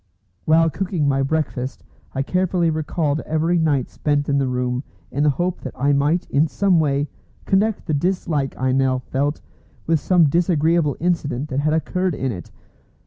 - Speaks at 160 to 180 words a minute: Yes, average, 170 wpm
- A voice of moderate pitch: Yes, medium, 150 Hz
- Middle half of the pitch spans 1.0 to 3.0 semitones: No, average, 3.5 semitones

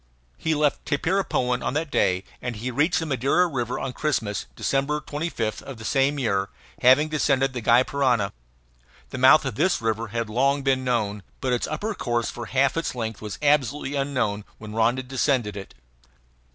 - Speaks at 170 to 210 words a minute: Yes, average, 180 wpm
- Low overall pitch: Yes, low, 130 Hz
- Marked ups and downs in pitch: No, average, 3.9 semitones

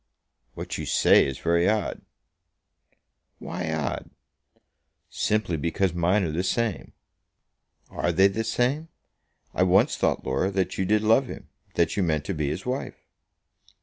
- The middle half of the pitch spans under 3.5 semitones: No, average, 4.3 semitones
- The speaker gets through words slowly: No, average, 150 wpm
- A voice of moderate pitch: No, very low, 95 Hz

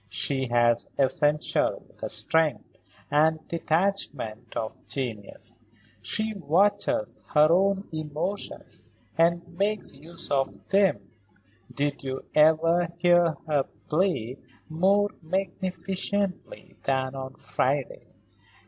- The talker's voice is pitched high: No, medium, 160 Hz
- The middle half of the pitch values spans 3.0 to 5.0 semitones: No, wide, 5.5 semitones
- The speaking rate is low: Yes, slow, 95 wpm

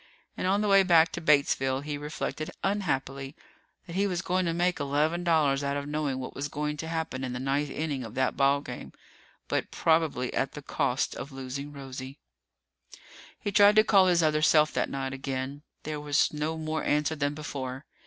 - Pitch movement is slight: No, average, 3.0 semitones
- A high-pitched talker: No, medium, 150 Hz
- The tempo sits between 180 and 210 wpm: Yes, average, 195 wpm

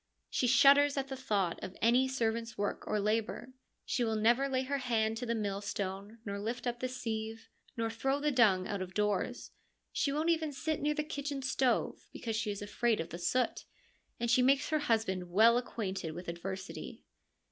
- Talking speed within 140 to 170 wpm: No, average, 190 wpm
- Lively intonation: No, average, 4.3 semitones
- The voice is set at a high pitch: Yes, high, 230 Hz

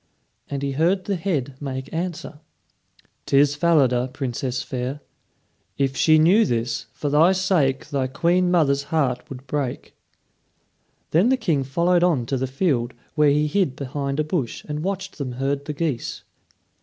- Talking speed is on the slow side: No, average, 155 wpm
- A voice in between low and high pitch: Yes, medium, 145 Hz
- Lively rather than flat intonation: No, average, 4.2 semitones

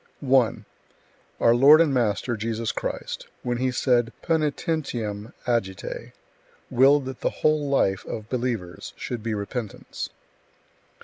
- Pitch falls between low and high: No, low, 120 Hz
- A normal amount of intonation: Yes, average, 3.6 semitones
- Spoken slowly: Yes, slow, 120 wpm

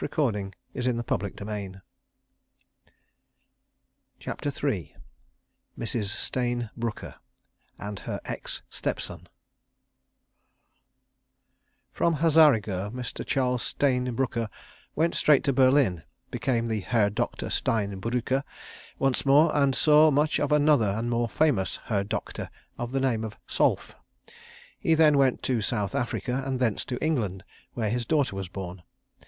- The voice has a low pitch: Yes, low, 120 Hz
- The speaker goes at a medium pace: No, slow, 125 wpm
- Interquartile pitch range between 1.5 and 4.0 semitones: No, average, 4.7 semitones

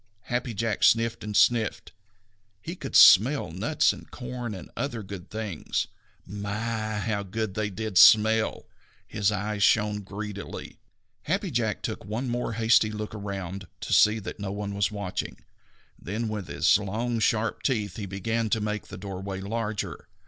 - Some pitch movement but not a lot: No, narrow, 2.1 semitones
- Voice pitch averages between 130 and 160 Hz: No, low, 105 Hz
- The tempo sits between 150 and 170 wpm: Yes, average, 155 wpm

